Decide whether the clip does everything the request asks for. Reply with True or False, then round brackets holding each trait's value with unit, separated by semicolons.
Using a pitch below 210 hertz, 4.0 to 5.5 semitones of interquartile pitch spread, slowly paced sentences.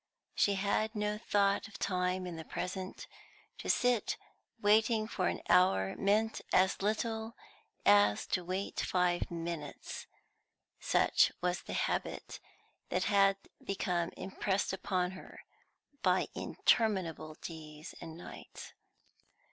False (190 Hz; 2.9 semitones; 115 wpm)